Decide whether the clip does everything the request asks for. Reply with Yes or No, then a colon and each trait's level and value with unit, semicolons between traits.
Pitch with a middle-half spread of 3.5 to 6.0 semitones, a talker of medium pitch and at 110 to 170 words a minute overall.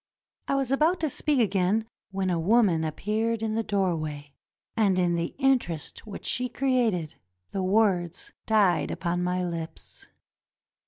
No: average, 4.7 semitones; high, 195 Hz; average, 145 wpm